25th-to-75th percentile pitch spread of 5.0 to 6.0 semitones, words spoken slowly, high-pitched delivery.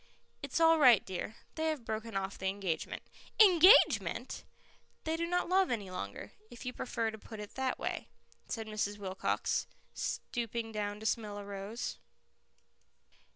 No: average, 5.3 semitones; average, 155 wpm; high, 220 Hz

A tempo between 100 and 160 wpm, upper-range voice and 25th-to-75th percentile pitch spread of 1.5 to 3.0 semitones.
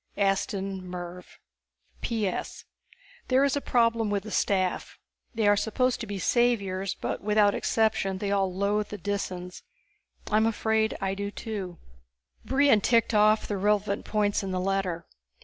Yes: average, 150 wpm; high, 205 Hz; narrow, 2.4 semitones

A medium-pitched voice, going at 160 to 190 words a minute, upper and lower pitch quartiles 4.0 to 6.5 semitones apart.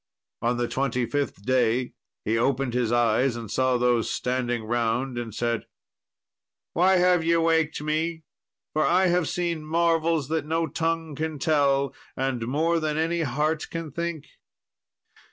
No: medium, 145 Hz; average, 150 wpm; average, 4.9 semitones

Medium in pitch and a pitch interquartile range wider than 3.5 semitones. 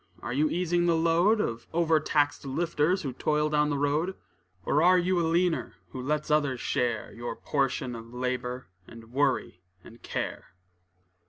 Yes: medium, 150 Hz; average, 4.8 semitones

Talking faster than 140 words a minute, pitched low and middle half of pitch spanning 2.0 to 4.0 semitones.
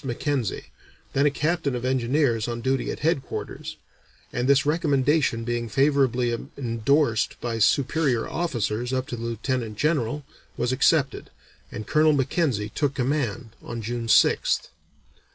No: slow, 135 wpm; low, 130 Hz; average, 3.6 semitones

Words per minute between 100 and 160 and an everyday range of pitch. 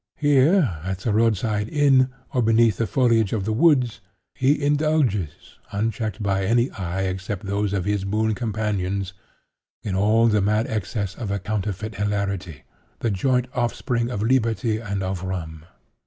Yes: average, 155 wpm; average, 3.3 semitones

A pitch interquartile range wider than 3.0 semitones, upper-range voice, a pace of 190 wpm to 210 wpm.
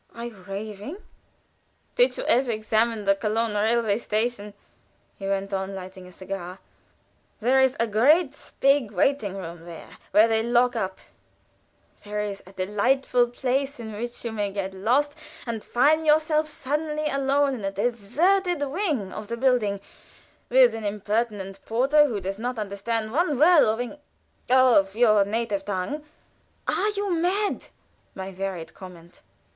No: average, 5.2 semitones; high, 230 Hz; average, 150 wpm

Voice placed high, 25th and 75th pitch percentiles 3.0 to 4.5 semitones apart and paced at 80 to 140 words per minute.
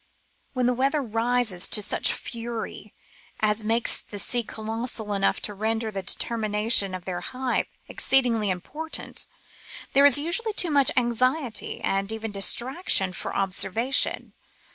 Yes: high, 225 Hz; average, 3.5 semitones; slow, 135 wpm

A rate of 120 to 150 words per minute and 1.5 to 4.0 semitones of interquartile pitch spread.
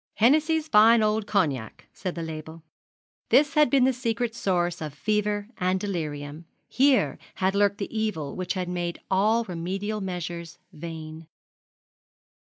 No: average, 140 wpm; average, 4.7 semitones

